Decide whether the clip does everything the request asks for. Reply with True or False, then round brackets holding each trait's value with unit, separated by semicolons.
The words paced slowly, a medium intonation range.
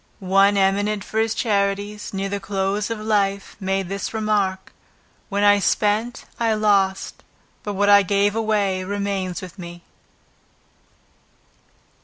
False (130 wpm; 1.4 semitones)